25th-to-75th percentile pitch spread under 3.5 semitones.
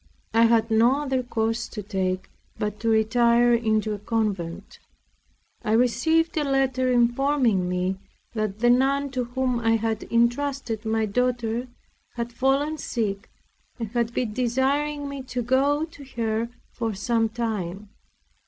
Yes: average, 3.0 semitones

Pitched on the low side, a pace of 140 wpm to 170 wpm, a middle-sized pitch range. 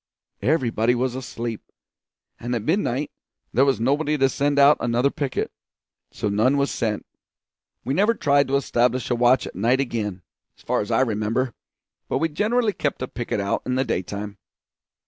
Yes: low, 130 Hz; average, 165 wpm; average, 3.5 semitones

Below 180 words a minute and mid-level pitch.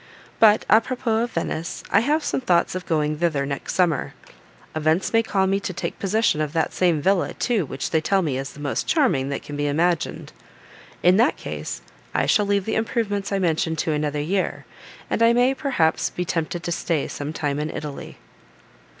No: average, 200 wpm; medium, 175 Hz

